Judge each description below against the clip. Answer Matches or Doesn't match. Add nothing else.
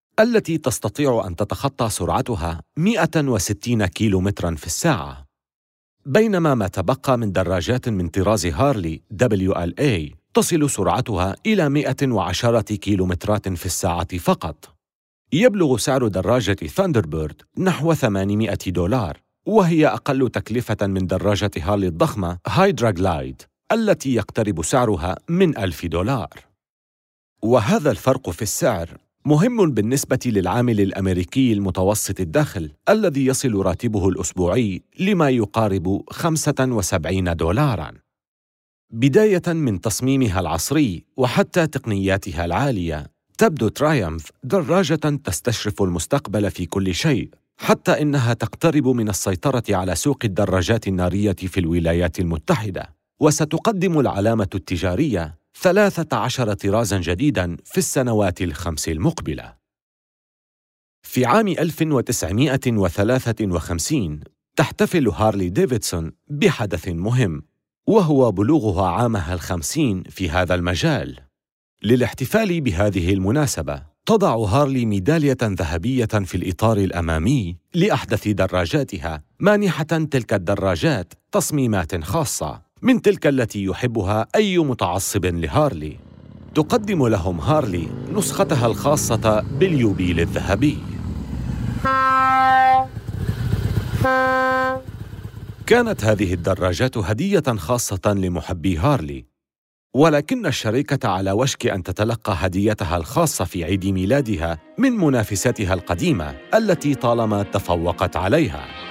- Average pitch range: Doesn't match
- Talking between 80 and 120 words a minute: Matches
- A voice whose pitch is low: Matches